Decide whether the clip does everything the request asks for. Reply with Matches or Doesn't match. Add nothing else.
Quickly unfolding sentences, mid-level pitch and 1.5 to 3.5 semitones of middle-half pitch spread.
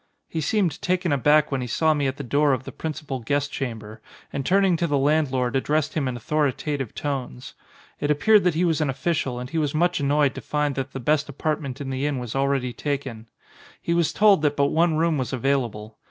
Matches